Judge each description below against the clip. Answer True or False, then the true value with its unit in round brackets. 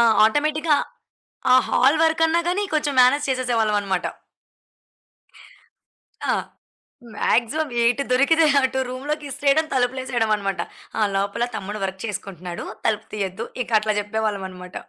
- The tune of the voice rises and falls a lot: True (5.9 semitones)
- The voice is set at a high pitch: True (240 Hz)